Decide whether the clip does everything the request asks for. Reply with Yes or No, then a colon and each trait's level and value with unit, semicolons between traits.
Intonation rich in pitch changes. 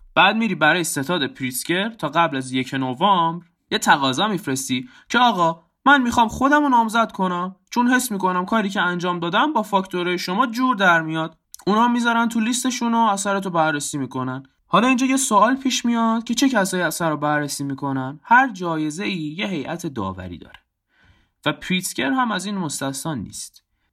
Yes: wide, 7.3 semitones